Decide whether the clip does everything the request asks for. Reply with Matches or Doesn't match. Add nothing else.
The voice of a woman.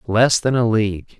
Doesn't match